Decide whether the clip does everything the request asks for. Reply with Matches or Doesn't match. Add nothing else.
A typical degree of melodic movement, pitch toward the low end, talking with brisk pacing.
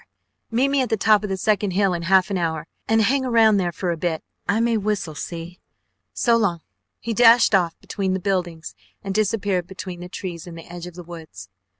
Doesn't match